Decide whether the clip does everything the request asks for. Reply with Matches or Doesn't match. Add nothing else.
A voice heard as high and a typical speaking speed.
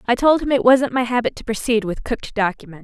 Doesn't match